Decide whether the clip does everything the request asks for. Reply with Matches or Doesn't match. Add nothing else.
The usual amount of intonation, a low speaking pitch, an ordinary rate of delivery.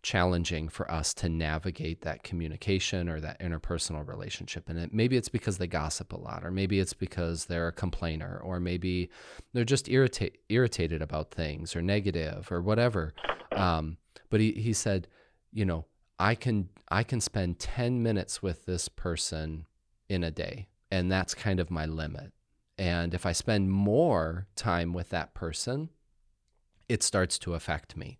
Matches